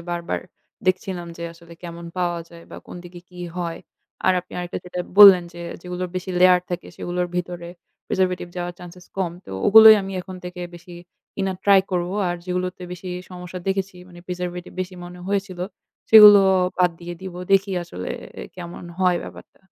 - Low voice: No, medium, 180 Hz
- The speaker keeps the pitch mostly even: Yes, narrow, 1.1 semitones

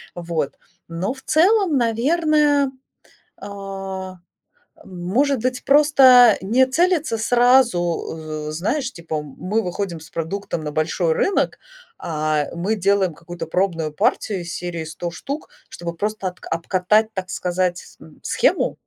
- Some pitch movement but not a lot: No, wide, 6.8 semitones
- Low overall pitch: No, high, 190 Hz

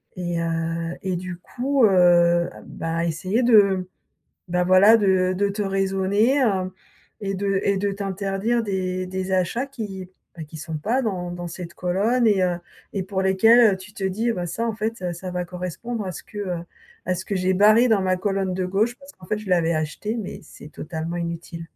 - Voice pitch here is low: No, high, 190 Hz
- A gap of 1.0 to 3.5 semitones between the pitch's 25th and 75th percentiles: Yes, average, 2.7 semitones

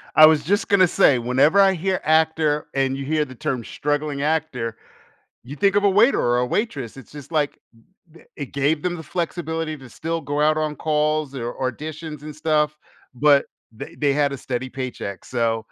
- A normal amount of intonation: Yes, average, 3.1 semitones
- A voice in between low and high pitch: Yes, medium, 150 Hz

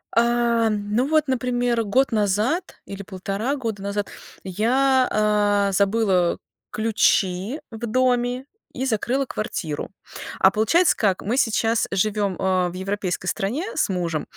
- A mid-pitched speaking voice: No, high, 215 Hz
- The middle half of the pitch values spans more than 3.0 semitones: Yes, average, 3.9 semitones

